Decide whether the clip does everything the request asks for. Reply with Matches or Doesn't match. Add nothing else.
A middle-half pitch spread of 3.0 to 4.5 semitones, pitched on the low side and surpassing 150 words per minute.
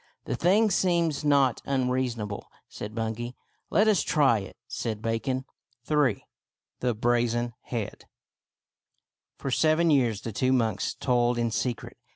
Doesn't match